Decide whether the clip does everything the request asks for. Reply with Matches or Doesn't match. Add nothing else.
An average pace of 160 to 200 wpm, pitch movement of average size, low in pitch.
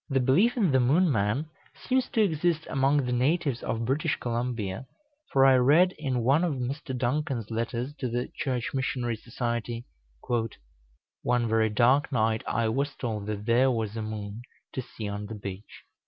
Matches